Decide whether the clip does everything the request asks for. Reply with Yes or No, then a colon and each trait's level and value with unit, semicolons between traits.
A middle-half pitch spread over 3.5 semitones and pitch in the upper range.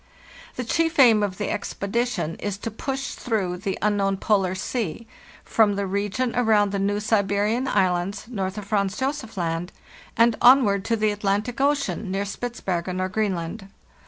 No: average, 3.1 semitones; high, 205 Hz